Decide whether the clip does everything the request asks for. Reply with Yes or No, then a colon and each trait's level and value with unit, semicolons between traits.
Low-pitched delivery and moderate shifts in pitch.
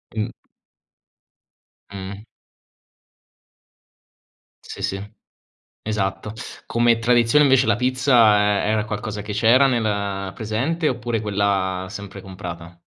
Yes: low, 105 Hz; average, 3.1 semitones